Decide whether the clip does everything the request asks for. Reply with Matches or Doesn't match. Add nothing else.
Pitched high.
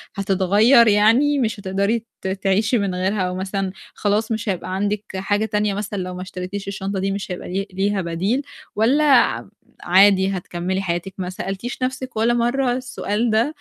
Matches